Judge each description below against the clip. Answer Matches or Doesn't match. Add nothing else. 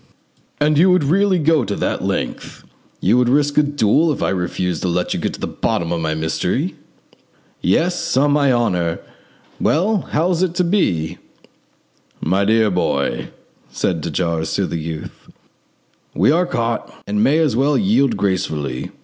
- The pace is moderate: Matches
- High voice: Doesn't match